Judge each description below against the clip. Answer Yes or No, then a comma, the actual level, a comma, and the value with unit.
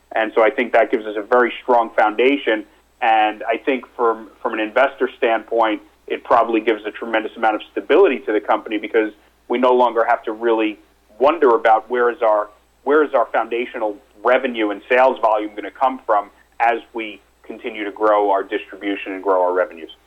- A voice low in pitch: Yes, low, 110 Hz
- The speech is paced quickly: No, average, 195 wpm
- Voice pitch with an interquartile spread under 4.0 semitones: Yes, narrow, 2.5 semitones